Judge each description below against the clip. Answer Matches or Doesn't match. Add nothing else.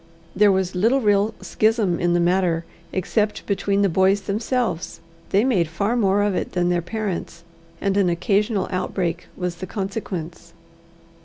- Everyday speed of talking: Matches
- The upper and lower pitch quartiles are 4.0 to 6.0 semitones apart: Doesn't match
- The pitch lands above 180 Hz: Matches